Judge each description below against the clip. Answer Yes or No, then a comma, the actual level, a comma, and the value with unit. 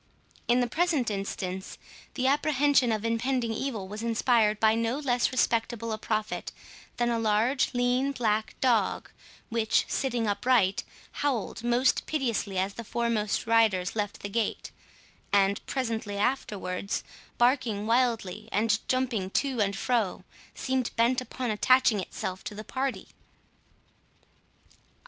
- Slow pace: Yes, slow, 130 wpm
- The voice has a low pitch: No, high, 230 Hz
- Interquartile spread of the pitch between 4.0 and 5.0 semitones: No, average, 3.3 semitones